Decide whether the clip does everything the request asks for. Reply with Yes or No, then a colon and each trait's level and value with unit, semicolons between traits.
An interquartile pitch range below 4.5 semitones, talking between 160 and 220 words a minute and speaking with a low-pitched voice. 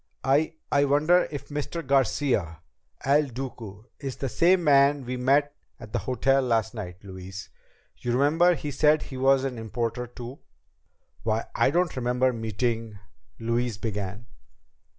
No: average, 4.1 semitones; average, 150 wpm; low, 130 Hz